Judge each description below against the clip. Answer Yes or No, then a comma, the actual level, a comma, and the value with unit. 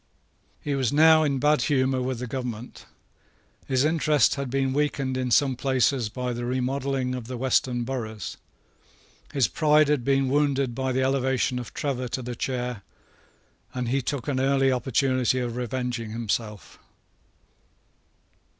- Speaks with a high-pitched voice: No, low, 130 Hz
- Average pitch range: No, narrow, 1.9 semitones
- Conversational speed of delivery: Yes, average, 150 wpm